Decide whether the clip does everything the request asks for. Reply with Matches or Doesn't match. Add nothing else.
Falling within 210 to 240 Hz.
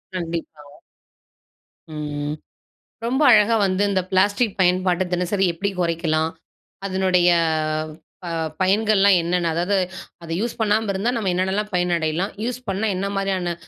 Doesn't match